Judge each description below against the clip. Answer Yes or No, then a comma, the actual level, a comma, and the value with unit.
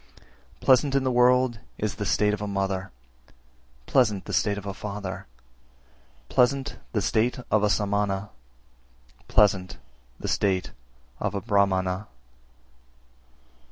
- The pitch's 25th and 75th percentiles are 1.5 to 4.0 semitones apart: Yes, average, 3.3 semitones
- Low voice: Yes, low, 105 Hz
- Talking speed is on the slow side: Yes, slow, 125 wpm